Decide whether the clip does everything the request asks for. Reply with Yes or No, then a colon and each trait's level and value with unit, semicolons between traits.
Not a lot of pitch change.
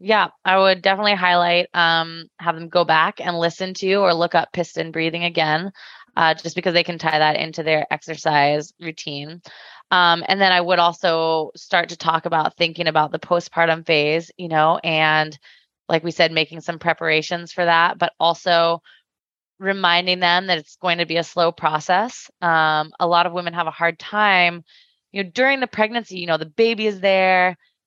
Yes: narrow, 1.9 semitones